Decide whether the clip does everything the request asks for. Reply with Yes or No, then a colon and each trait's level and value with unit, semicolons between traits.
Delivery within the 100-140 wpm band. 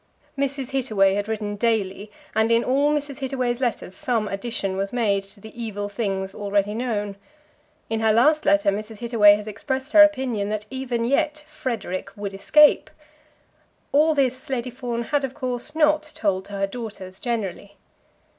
No: average, 165 wpm